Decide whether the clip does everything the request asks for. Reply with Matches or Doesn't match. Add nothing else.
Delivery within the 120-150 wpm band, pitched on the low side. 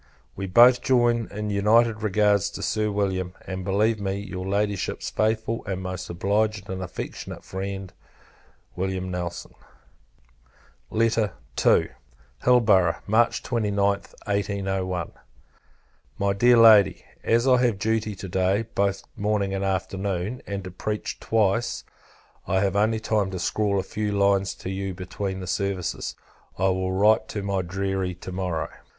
Matches